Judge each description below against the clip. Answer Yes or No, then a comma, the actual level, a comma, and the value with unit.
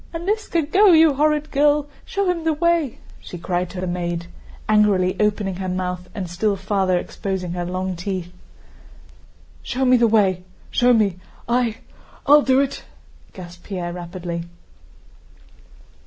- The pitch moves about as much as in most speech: No, wide, 7.6 semitones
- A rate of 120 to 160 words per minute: Yes, average, 140 wpm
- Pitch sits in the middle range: No, high, 200 Hz